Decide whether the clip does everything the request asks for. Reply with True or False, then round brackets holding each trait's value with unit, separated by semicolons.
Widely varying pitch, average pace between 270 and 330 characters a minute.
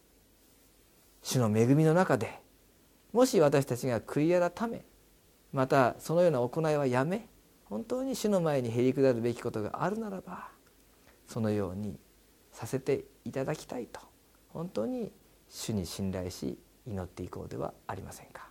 True (8.0 semitones; 285 characters per minute)